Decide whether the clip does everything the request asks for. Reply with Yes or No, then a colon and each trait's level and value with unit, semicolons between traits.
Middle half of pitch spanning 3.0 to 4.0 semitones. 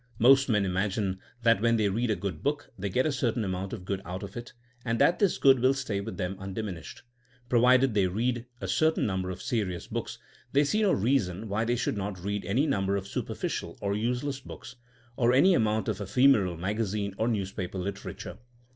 No: average, 4.5 semitones